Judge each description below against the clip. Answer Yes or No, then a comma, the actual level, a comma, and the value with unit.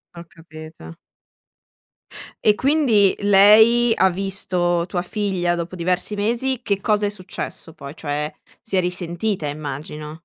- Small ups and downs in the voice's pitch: No, average, 4.0 semitones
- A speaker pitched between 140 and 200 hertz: Yes, medium, 185 Hz